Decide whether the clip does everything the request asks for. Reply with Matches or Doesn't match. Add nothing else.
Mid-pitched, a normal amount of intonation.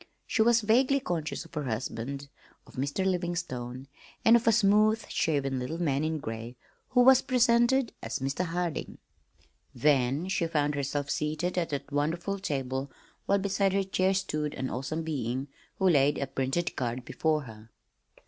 Doesn't match